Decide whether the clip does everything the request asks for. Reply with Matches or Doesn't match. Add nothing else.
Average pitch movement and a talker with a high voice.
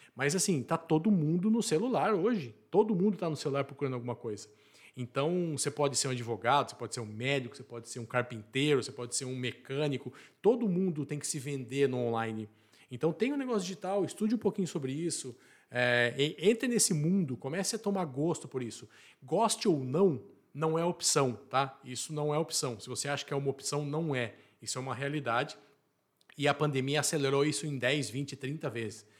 Doesn't match